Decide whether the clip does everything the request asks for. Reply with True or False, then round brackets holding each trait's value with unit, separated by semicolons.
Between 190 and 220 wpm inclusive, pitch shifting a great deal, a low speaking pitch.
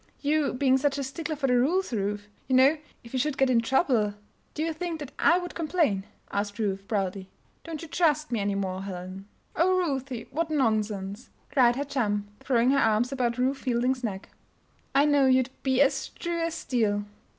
False (195 wpm; 5.8 semitones; 260 Hz)